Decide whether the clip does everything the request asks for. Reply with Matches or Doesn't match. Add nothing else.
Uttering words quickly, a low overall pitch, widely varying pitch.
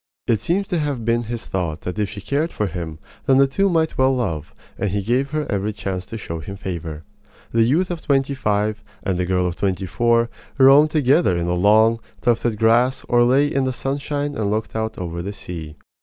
Matches